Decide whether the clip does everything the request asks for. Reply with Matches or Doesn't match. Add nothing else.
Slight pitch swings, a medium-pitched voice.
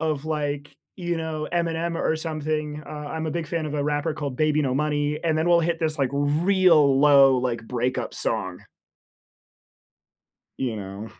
Matches